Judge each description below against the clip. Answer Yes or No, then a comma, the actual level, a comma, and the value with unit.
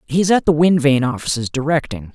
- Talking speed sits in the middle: No, fast, 225 wpm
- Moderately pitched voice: Yes, medium, 145 Hz